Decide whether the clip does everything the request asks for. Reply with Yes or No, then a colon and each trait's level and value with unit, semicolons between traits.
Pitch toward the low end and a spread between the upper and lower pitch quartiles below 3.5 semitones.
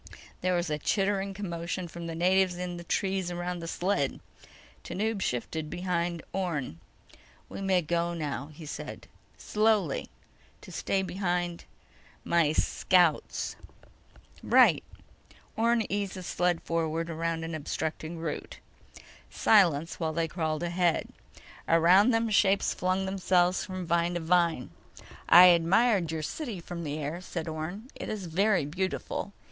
No: medium, 175 Hz; narrow, 2.6 semitones